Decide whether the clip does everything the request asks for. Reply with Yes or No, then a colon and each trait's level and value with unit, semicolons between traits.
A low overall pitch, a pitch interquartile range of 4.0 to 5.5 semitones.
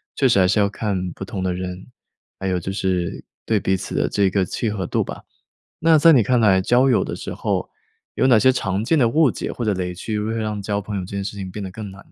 No: low, 100 Hz; average, 3.3 semitones